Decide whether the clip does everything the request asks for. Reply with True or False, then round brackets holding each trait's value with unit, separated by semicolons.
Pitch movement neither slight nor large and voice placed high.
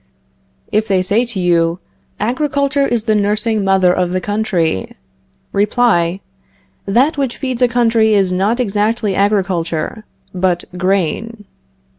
True (4.0 semitones; 205 Hz)